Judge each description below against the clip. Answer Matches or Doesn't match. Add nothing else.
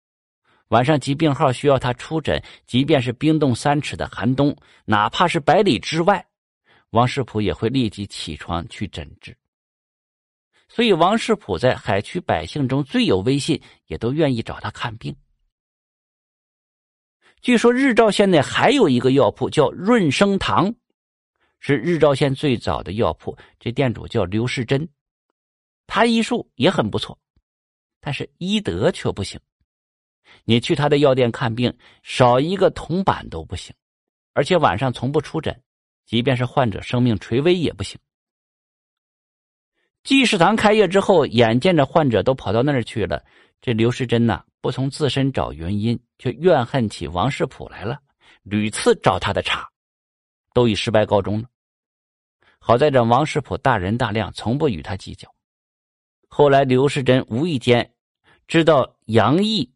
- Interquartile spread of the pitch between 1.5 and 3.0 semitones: Doesn't match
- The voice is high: Doesn't match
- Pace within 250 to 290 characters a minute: Doesn't match